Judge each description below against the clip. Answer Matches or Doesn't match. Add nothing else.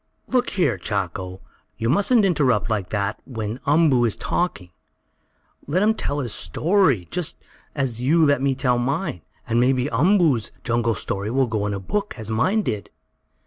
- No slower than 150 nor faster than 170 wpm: Matches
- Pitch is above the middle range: Doesn't match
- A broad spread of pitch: Matches